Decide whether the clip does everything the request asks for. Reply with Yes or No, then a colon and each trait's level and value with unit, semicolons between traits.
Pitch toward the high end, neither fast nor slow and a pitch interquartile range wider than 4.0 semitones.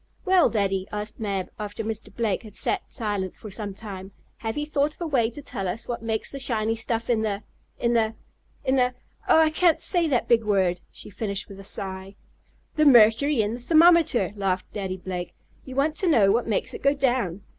No: high, 225 Hz; fast, 210 wpm; average, 5.0 semitones